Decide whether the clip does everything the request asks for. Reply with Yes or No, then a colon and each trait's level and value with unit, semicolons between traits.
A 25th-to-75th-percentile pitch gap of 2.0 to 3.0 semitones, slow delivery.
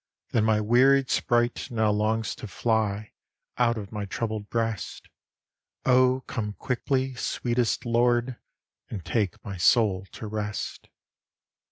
Yes: narrow, 2.5 semitones; slow, 125 wpm